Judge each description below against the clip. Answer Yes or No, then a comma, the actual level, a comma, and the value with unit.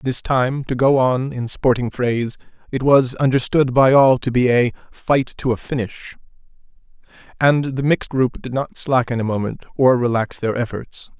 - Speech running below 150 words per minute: No, average, 175 wpm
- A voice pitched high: No, low, 125 Hz